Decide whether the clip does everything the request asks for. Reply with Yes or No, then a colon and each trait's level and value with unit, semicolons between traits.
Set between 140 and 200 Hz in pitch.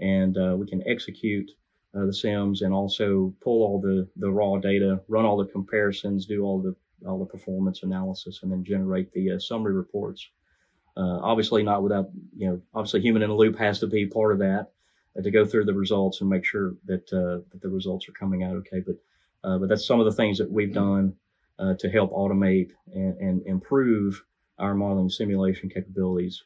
No: very low, 95 Hz